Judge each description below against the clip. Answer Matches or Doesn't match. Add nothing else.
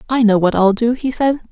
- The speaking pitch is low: Doesn't match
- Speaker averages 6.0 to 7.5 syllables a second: Doesn't match